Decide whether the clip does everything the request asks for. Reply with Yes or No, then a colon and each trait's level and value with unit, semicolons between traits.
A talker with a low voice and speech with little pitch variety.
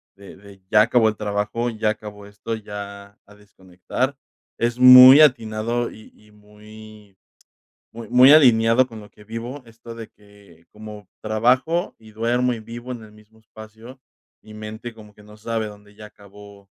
Yes: low, 110 Hz; narrow, 2.1 semitones